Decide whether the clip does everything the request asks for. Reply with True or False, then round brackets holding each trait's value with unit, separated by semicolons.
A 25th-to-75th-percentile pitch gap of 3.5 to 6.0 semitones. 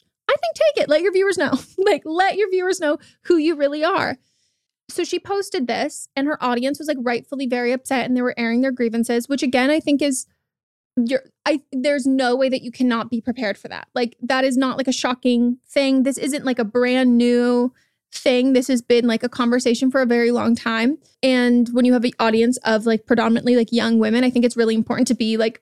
False (2.7 semitones)